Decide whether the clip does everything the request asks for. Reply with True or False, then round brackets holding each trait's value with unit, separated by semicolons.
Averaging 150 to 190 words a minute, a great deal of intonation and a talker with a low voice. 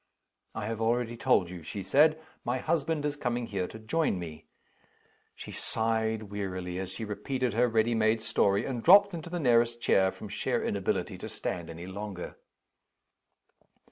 False (165 wpm; 4.1 semitones; 110 Hz)